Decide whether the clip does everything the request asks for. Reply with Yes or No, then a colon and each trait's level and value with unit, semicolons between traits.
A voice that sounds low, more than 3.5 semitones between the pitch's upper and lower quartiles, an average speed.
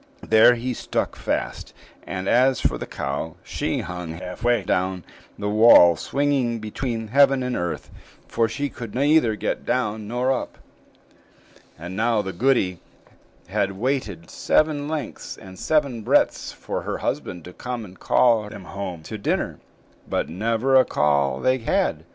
Yes: low, 110 Hz; wide, 5.5 semitones; average, 155 wpm